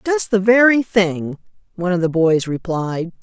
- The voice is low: No, high, 190 Hz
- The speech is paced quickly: No, average, 165 wpm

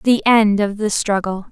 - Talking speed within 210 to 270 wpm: No, average, 200 wpm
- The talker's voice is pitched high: Yes, high, 210 Hz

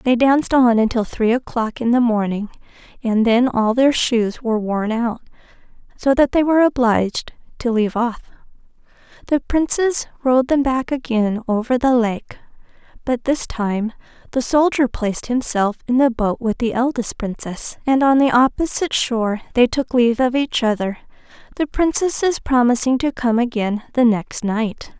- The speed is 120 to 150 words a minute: No, average, 165 wpm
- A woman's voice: Yes, female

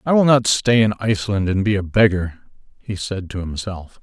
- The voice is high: No, low, 100 Hz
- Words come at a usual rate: No, fast, 210 wpm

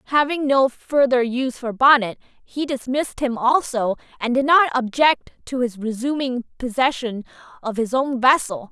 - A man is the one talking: No, female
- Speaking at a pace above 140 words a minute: Yes, average, 150 wpm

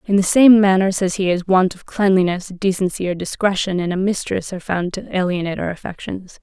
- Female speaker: Yes, female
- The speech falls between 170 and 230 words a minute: Yes, fast, 205 wpm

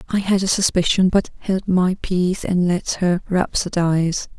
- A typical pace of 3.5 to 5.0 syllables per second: Yes, 4.6 syllables/s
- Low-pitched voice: No, medium, 180 Hz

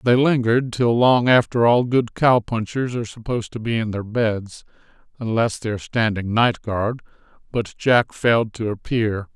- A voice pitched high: No, low, 115 Hz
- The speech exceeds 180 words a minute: No, average, 155 wpm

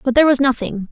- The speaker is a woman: Yes, female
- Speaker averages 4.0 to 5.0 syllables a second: No, 7.4 syllables/s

